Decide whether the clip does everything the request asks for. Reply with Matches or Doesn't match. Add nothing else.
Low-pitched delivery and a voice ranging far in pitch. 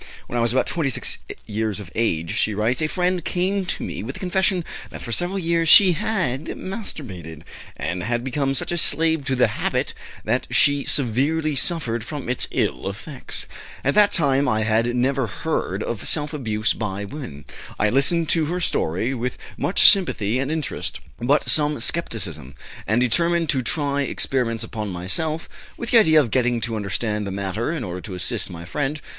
Matches